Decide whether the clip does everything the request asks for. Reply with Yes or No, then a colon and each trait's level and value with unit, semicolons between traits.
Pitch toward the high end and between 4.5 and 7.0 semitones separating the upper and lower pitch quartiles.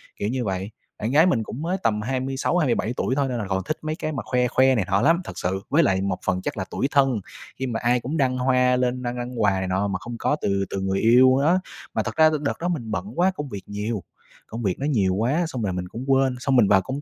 No: low, 125 Hz; average, 5.0 semitones